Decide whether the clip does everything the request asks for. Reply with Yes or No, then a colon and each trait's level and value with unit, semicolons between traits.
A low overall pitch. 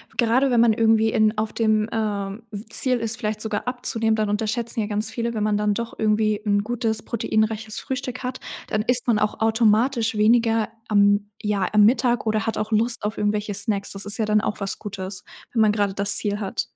No: high, 215 Hz